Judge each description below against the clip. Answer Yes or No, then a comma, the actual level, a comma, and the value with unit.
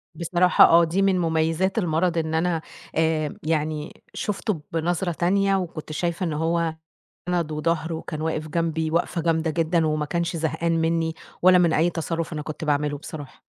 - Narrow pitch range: Yes, narrow, 1.6 semitones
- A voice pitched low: No, medium, 165 Hz